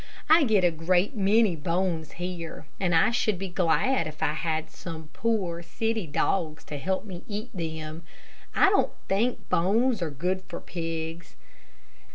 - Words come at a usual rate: Yes, average, 160 wpm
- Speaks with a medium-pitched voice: Yes, medium, 175 Hz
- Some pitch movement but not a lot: Yes, average, 4.2 semitones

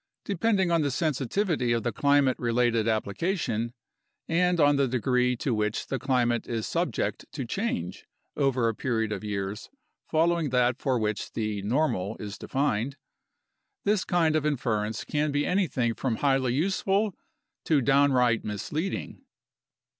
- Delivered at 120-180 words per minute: Yes, average, 145 wpm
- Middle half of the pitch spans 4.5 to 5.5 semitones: Yes, average, 5.1 semitones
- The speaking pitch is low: Yes, low, 130 Hz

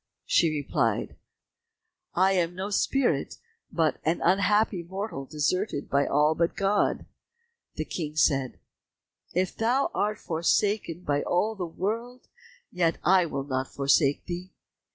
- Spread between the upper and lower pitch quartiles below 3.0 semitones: No, average, 4.7 semitones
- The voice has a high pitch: No, medium, 175 Hz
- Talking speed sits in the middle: No, slow, 130 wpm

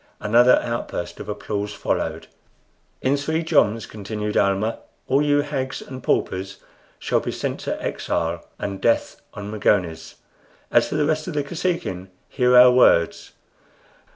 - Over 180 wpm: No, average, 145 wpm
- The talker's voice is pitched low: Yes, low, 115 Hz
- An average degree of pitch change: No, wide, 6.1 semitones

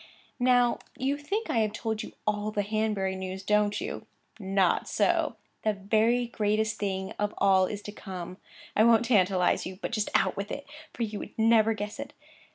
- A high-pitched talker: Yes, high, 210 Hz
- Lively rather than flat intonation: No, narrow, 2.4 semitones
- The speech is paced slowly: No, average, 185 wpm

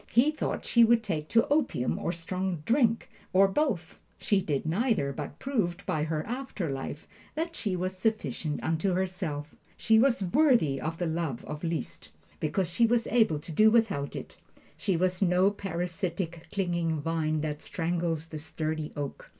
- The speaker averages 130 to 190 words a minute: Yes, average, 165 wpm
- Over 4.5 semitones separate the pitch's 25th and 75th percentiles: Yes, wide, 5.6 semitones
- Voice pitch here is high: No, medium, 175 Hz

